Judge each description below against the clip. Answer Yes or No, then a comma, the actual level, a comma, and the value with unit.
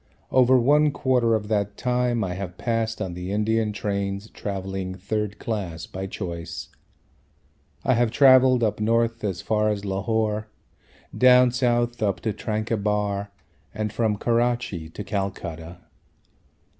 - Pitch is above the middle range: No, low, 105 Hz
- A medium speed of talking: No, slow, 130 wpm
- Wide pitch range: No, average, 3.2 semitones